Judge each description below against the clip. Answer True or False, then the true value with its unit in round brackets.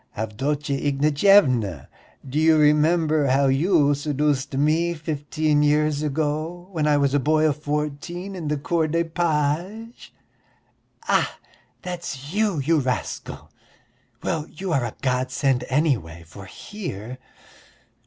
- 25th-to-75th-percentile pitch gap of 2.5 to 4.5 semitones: True (2.9 semitones)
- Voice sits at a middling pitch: True (150 Hz)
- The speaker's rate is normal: False (125 wpm)